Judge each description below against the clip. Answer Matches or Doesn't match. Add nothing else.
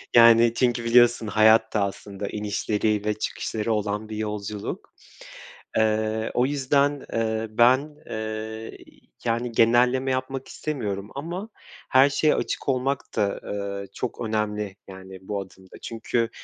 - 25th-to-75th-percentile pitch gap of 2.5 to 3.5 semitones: Matches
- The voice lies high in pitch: Doesn't match